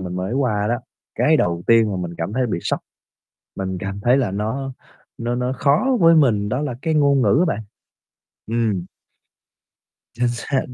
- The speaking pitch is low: Yes, low, 120 Hz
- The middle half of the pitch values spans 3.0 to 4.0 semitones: No, average, 5.2 semitones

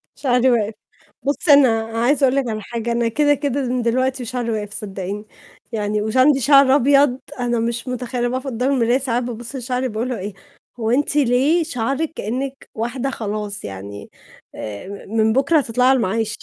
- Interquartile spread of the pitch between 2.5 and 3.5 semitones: Yes, average, 3.2 semitones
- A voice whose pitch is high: Yes, high, 245 Hz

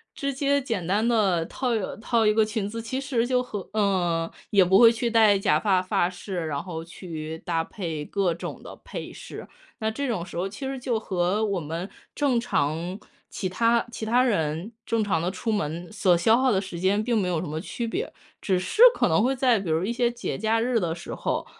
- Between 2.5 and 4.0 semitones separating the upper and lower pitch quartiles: No, average, 5.0 semitones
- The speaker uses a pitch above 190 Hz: Yes, high, 205 Hz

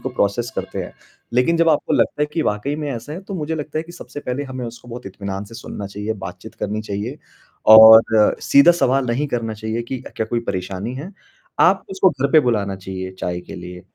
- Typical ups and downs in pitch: No, wide, 6.0 semitones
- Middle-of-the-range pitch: No, low, 120 Hz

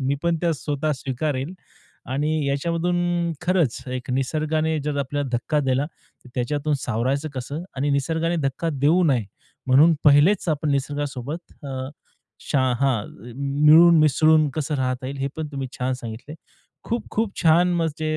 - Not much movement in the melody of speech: No, average, 3.2 semitones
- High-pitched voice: No, medium, 145 Hz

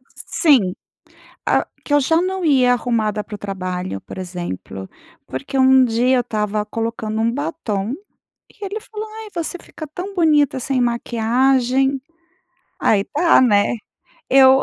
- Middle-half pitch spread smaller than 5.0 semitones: No, wide, 5.5 semitones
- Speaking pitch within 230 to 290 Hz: Yes, very high, 250 Hz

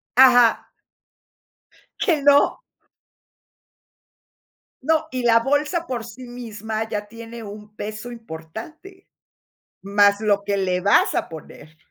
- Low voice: No, high, 225 Hz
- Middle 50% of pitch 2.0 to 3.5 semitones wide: No, average, 4.0 semitones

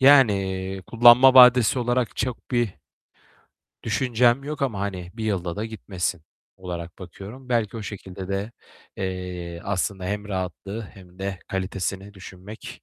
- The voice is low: Yes, low, 100 Hz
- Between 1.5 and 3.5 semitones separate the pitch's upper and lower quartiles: No, average, 4.2 semitones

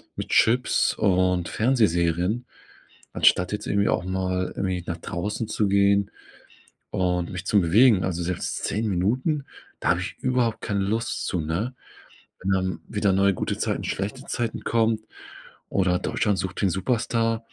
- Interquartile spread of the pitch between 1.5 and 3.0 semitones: No, average, 3.7 semitones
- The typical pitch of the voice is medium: No, low, 100 Hz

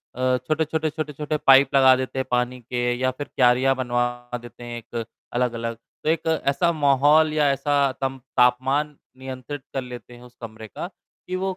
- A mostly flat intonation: No, average, 3.0 semitones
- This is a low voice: Yes, low, 130 Hz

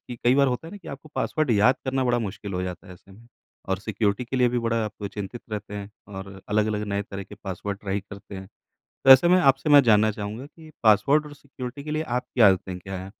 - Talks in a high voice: No, low, 110 Hz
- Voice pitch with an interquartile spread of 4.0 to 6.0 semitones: Yes, average, 4.7 semitones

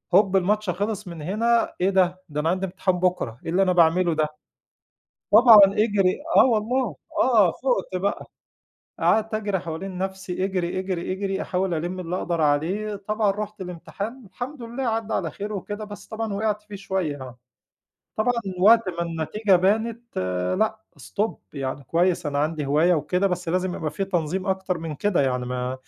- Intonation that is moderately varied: Yes, average, 3.6 semitones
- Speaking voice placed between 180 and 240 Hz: Yes, high, 190 Hz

